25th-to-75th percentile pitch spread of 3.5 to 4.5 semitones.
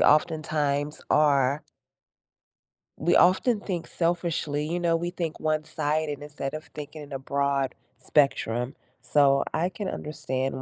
No: average, 2.8 semitones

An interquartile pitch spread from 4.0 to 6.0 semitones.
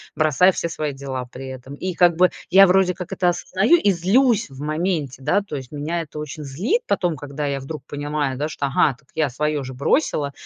Yes: average, 4.5 semitones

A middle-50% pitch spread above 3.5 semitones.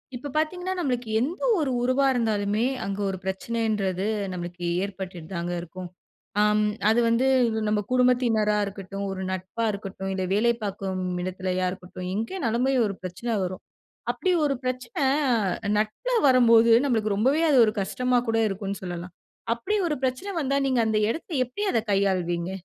Yes: average, 4.9 semitones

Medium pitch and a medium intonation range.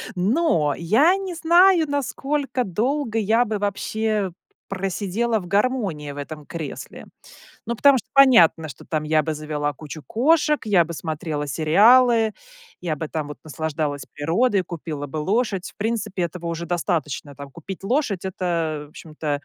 No: medium, 180 Hz; wide, 7.0 semitones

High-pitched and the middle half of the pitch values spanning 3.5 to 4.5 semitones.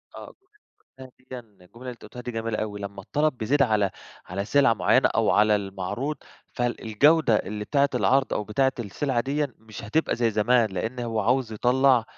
No: low, 115 Hz; average, 3.9 semitones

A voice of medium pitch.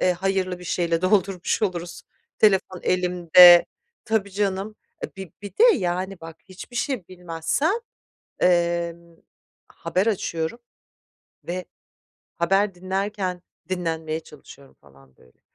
Yes: medium, 180 Hz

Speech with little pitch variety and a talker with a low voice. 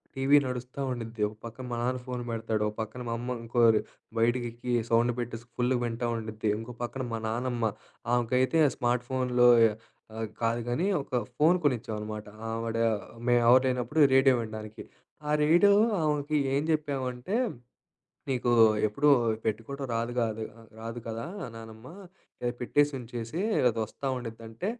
Yes: narrow, 2.3 semitones; low, 120 Hz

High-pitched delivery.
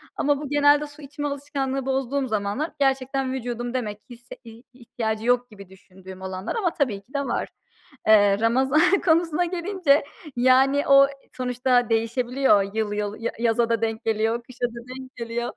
Yes: very high, 250 Hz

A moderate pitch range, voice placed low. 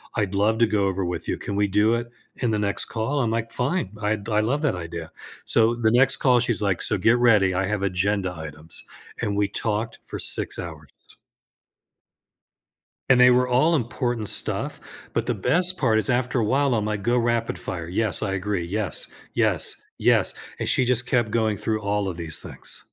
Yes: average, 3.6 semitones; low, 110 Hz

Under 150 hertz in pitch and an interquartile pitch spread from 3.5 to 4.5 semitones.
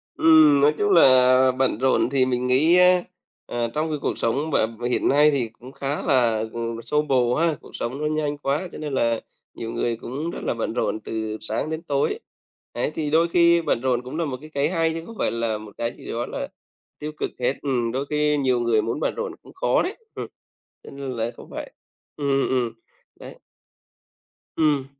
Yes: low, 135 Hz; average, 4.2 semitones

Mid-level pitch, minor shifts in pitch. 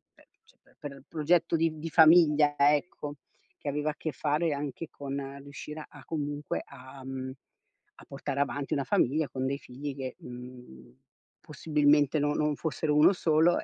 Yes: medium, 145 Hz; narrow, 2.0 semitones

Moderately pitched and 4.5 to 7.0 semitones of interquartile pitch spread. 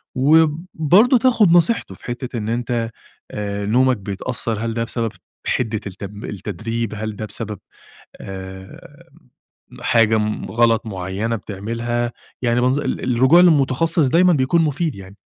No: low, 115 Hz; average, 5.0 semitones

